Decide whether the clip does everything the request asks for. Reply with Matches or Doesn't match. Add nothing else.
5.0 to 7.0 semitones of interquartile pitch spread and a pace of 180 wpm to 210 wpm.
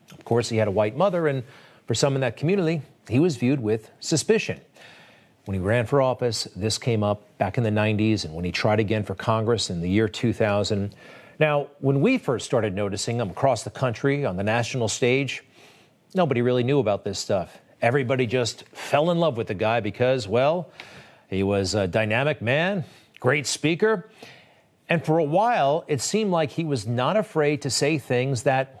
Matches